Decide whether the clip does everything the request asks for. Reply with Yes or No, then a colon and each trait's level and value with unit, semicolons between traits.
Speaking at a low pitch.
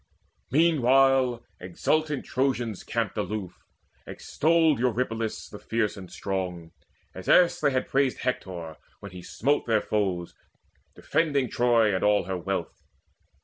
Yes: low, 115 Hz